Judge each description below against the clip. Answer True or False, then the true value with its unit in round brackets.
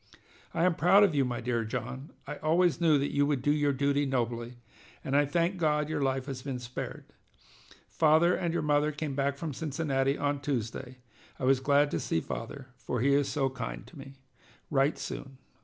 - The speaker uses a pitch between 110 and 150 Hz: True (140 Hz)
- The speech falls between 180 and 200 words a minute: True (195 wpm)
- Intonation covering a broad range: False (2.4 semitones)